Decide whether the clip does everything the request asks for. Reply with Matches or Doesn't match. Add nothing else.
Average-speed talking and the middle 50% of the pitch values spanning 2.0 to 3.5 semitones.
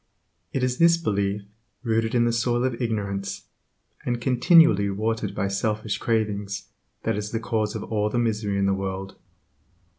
Matches